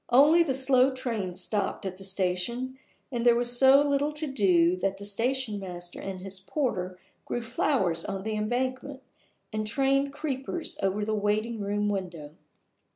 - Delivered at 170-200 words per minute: No, average, 160 wpm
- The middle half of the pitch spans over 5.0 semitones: Yes, wide, 5.4 semitones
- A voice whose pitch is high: Yes, high, 220 Hz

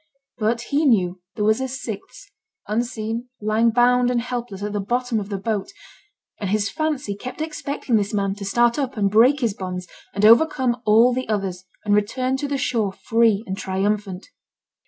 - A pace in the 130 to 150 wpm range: No, average, 180 wpm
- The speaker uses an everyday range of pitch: Yes, average, 3.5 semitones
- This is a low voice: No, high, 225 Hz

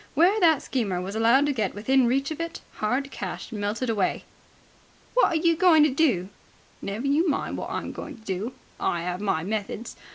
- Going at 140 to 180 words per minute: No, average, 195 wpm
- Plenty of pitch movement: Yes, wide, 6.7 semitones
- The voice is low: No, high, 245 Hz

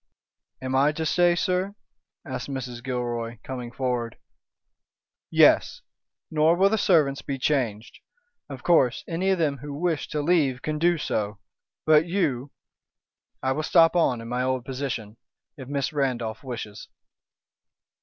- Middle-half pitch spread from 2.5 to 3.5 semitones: No, average, 4.6 semitones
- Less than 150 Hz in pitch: Yes, low, 135 Hz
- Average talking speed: Yes, average, 145 wpm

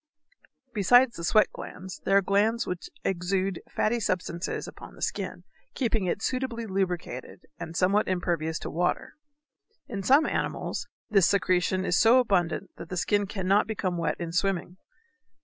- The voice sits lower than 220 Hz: Yes, high, 190 Hz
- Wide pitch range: No, average, 3.1 semitones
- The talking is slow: No, average, 150 wpm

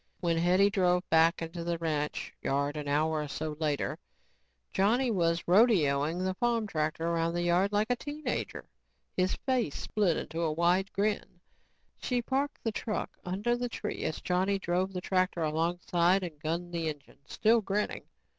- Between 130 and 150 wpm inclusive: No, average, 170 wpm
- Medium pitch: Yes, medium, 180 Hz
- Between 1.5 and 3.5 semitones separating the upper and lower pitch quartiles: No, average, 3.9 semitones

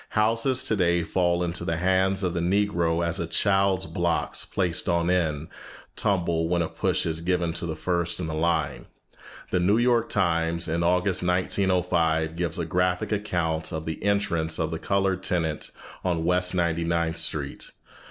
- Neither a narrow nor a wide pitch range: No, narrow, 2.1 semitones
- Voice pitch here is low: Yes, very low, 85 Hz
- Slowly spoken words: No, average, 170 wpm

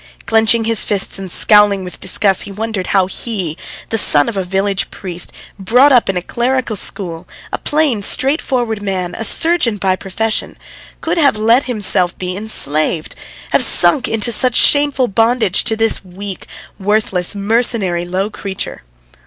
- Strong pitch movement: No, average, 3.7 semitones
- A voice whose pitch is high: Yes, high, 210 Hz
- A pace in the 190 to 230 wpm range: No, average, 160 wpm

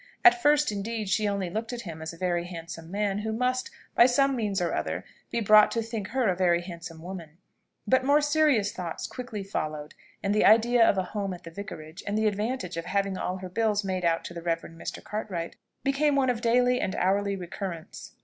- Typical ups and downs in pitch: Yes, average, 4.8 semitones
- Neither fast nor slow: No, fast, 215 wpm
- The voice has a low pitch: No, high, 200 Hz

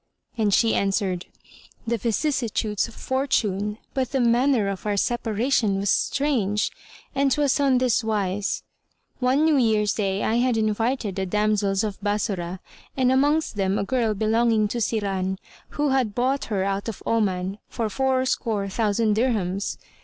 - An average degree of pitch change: Yes, average, 4.1 semitones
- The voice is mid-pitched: No, high, 220 Hz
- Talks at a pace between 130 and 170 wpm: Yes, average, 155 wpm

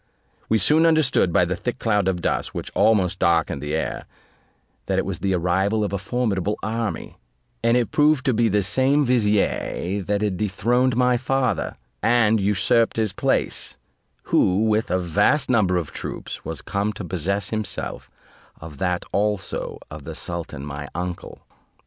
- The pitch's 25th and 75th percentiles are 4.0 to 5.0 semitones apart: Yes, average, 4.4 semitones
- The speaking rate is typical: Yes, average, 165 wpm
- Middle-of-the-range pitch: No, low, 105 Hz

